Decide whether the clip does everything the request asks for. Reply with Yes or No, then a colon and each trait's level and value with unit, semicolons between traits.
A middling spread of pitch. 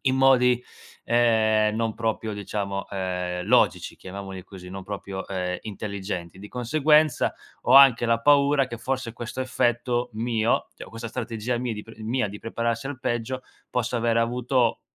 Yes: average, 3.3 semitones